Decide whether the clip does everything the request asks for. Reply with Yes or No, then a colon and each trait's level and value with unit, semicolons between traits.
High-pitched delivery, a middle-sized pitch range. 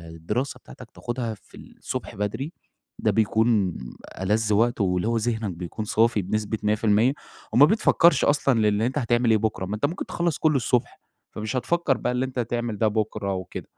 No: low, 115 Hz; average, 3.0 semitones